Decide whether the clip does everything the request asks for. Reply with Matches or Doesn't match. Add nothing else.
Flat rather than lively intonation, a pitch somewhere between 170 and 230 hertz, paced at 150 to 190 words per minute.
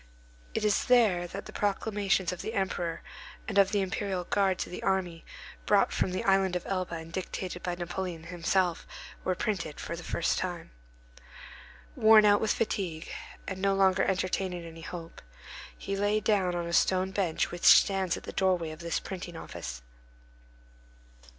Matches